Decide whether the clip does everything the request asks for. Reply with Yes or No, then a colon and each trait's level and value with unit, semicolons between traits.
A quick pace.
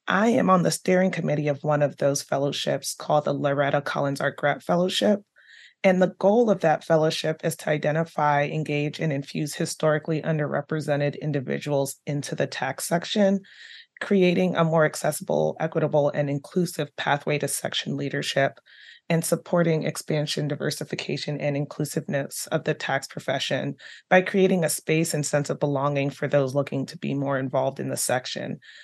No: average, 160 wpm